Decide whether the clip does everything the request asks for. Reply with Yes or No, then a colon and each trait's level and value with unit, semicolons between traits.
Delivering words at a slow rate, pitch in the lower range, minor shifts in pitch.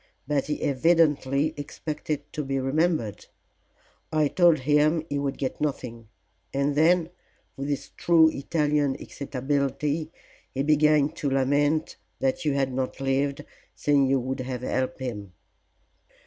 No: slow, 130 wpm; medium, 145 Hz; narrow, 2.2 semitones